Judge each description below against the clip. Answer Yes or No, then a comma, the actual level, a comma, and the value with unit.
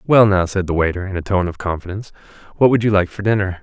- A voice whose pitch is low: Yes, very low, 95 Hz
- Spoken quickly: Yes, fast, 265 wpm